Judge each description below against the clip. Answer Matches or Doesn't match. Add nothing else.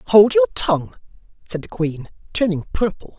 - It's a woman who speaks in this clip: Doesn't match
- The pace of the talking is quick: Doesn't match